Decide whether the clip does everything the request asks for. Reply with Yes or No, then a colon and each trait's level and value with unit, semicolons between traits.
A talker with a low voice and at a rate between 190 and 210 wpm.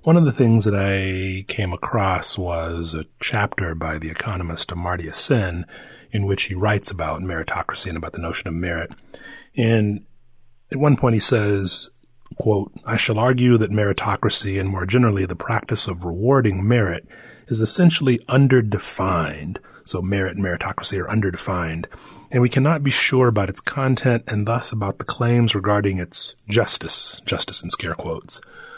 No: low, 105 Hz; average, 160 wpm